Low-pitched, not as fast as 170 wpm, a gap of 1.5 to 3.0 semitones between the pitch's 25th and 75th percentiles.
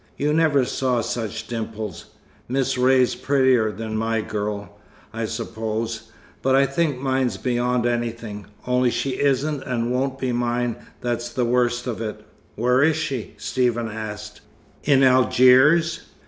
Yes: low, 125 Hz; average, 140 wpm; average, 2.7 semitones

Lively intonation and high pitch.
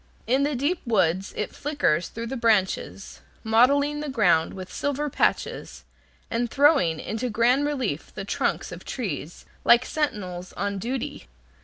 Yes: wide, 6.4 semitones; high, 235 Hz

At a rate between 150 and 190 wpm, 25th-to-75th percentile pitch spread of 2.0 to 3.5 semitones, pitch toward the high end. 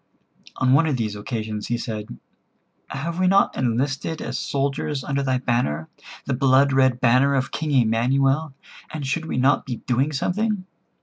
No: average, 165 wpm; average, 3.0 semitones; low, 135 Hz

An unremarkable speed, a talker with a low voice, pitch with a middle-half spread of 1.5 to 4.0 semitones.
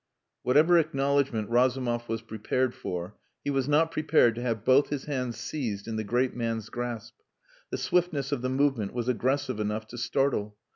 Yes: average, 175 wpm; low, 125 Hz; average, 3.7 semitones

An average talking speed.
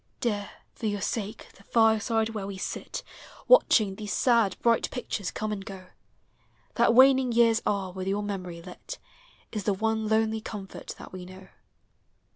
Yes: average, 160 wpm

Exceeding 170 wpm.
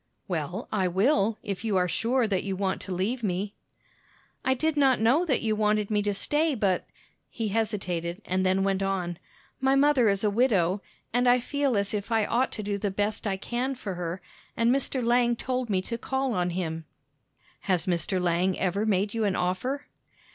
Yes: average, 200 wpm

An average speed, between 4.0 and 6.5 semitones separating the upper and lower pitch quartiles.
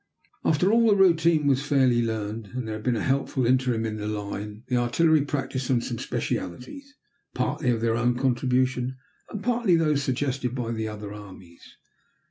Yes: average, 175 wpm; average, 4.3 semitones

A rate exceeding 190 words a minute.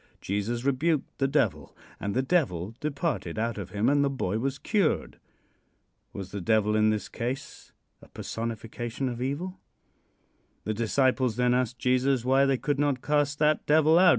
No: average, 165 wpm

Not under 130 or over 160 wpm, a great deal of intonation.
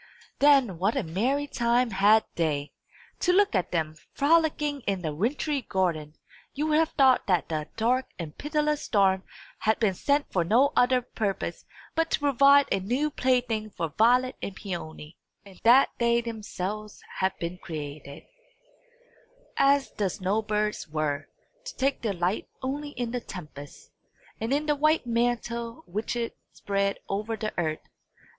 Yes: average, 155 wpm; wide, 6.6 semitones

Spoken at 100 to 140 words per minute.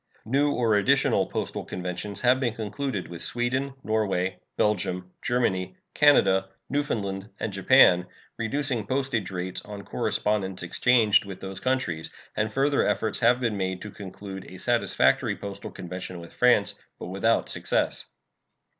Yes: slow, 135 wpm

